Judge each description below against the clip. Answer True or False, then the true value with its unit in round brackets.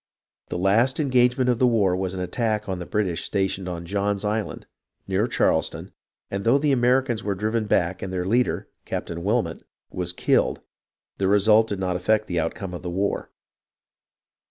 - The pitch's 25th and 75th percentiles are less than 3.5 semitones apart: False (3.8 semitones)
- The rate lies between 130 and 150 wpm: False (175 wpm)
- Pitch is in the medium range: False (100 Hz)